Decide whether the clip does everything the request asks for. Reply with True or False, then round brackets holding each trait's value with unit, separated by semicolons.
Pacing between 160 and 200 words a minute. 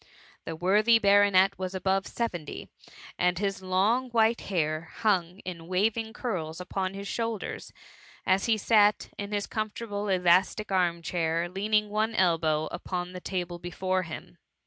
False (145 wpm)